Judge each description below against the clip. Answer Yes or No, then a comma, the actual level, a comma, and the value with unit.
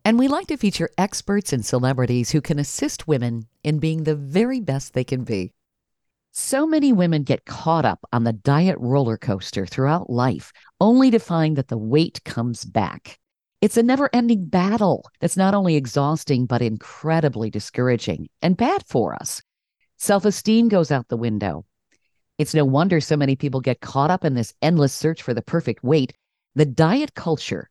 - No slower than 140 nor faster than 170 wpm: No, average, 180 wpm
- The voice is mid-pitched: Yes, medium, 150 Hz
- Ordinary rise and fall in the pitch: No, wide, 6.9 semitones